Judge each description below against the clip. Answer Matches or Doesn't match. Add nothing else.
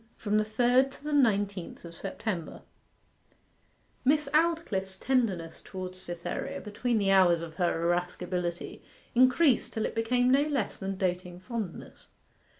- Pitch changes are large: Matches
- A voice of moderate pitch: Doesn't match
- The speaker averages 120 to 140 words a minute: Matches